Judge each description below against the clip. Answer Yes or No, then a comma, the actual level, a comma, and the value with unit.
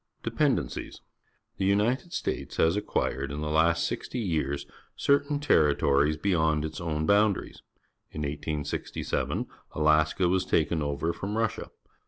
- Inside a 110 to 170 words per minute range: Yes, slow, 135 wpm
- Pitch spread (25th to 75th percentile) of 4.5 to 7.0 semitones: Yes, average, 4.9 semitones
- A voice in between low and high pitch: No, very low, 80 Hz